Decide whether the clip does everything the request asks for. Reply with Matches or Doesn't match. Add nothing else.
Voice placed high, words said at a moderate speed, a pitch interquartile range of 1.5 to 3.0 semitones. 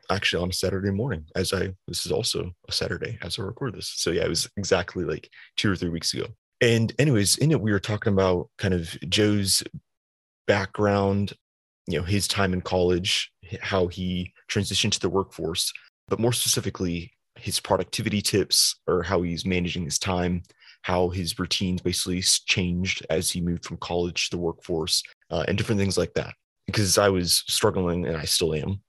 Doesn't match